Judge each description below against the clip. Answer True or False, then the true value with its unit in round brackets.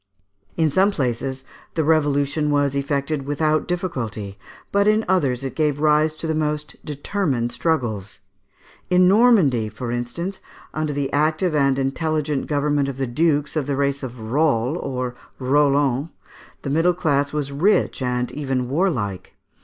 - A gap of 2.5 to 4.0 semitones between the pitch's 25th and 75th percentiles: True (3.1 semitones)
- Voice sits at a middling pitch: True (145 Hz)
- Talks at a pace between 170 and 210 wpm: False (145 wpm)